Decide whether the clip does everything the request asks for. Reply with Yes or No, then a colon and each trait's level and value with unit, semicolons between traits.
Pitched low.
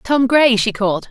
No: high, 235 Hz